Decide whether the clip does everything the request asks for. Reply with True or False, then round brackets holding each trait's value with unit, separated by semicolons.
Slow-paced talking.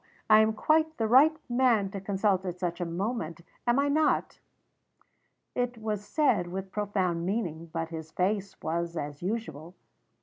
False (160 wpm)